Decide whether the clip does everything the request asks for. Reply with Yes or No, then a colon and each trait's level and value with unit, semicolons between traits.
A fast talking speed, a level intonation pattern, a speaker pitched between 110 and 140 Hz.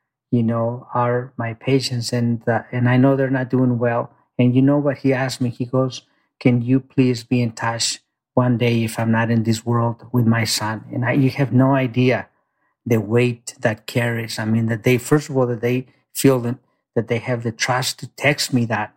Yes: fast, 220 wpm; narrow, 2.0 semitones; low, 125 Hz